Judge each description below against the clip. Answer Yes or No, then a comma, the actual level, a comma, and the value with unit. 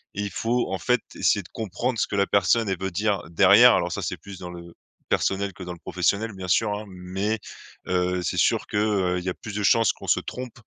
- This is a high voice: No, low, 100 Hz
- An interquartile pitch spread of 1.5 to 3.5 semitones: Yes, average, 2.9 semitones